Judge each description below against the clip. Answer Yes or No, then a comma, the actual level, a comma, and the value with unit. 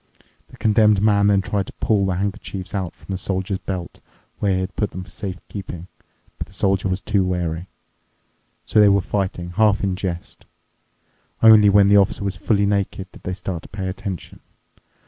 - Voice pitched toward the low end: Yes, very low, 95 Hz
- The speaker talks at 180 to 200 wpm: Yes, average, 190 wpm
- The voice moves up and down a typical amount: No, narrow, 1.7 semitones